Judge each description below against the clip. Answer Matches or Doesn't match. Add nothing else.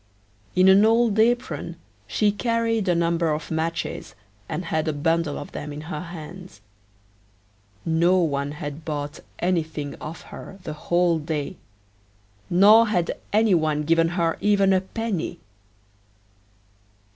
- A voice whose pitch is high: Doesn't match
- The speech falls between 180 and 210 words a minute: Doesn't match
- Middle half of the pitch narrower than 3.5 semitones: Doesn't match